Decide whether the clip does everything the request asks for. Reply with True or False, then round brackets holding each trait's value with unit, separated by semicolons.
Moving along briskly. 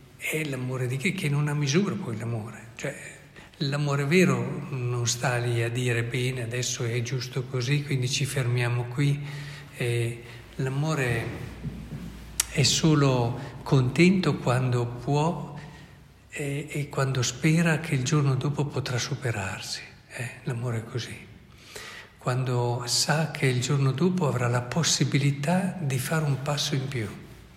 False (135 wpm)